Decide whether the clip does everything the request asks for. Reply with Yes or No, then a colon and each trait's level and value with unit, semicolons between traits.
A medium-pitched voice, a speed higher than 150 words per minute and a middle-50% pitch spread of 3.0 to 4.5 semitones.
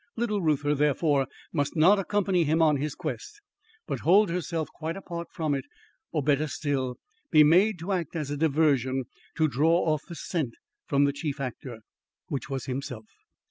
Yes: medium, 155 Hz; average, 175 wpm; average, 3.4 semitones